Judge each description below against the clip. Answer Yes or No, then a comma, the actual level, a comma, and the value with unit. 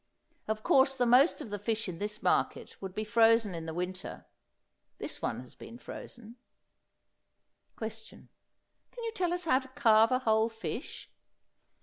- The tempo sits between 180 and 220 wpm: No, average, 160 wpm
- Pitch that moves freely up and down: No, average, 3.5 semitones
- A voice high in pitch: Yes, high, 225 Hz